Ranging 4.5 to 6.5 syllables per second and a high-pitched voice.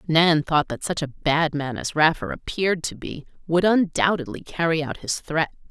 No: 4.8 syllables/s; medium, 160 Hz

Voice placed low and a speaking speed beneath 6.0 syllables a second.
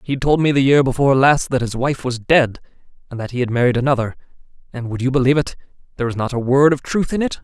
No: low, 130 Hz; 6.9 syllables/s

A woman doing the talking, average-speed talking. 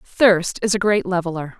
Yes: female; average, 190 wpm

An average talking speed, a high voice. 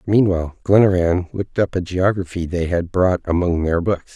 No: average, 175 wpm; very low, 90 Hz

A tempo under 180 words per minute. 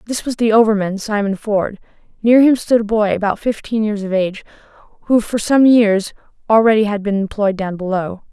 No: average, 190 wpm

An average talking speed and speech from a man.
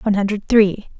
No: average, 180 wpm; female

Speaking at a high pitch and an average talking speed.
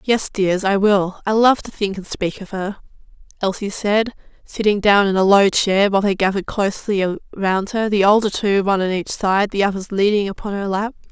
No: high, 200 Hz; fast, 210 wpm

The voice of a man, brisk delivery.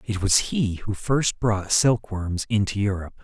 No: male; average, 185 wpm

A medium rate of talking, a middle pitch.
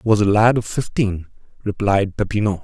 No: average, 160 wpm; low, 105 Hz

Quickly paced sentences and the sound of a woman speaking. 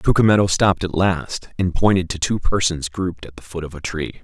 No: fast, 225 wpm; male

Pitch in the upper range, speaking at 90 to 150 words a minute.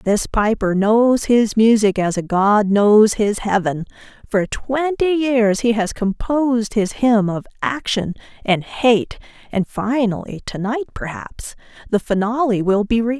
Yes: high, 220 Hz; average, 145 wpm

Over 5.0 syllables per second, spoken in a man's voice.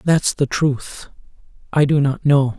No: 3.7 syllables/s; male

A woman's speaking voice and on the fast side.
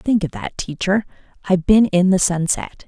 No: female; average, 190 wpm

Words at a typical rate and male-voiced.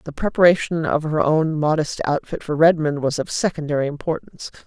No: average, 165 wpm; female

